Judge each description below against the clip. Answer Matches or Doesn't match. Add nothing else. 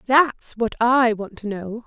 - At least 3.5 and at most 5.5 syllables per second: Matches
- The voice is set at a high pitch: Matches